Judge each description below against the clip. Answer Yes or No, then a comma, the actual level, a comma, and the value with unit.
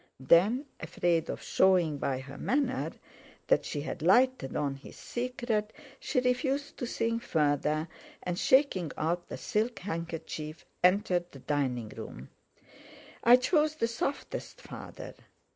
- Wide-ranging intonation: Yes, wide, 8.3 semitones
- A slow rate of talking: Yes, slow, 130 wpm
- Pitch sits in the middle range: Yes, medium, 180 Hz